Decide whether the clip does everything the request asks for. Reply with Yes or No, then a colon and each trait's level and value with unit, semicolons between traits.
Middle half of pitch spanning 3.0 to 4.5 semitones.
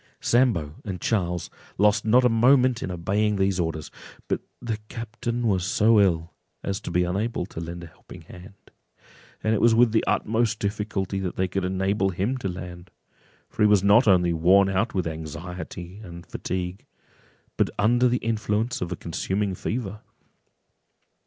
Yes: average, 3.8 semitones